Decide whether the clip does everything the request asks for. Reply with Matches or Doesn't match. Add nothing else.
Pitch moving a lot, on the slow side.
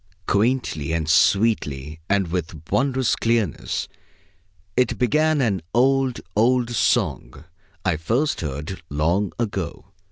Matches